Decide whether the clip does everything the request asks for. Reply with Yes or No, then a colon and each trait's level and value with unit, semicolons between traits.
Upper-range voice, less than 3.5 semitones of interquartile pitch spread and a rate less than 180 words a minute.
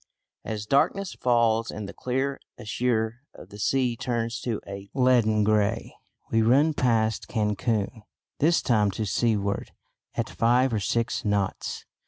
No: low, 115 Hz; average, 2.9 semitones; average, 140 wpm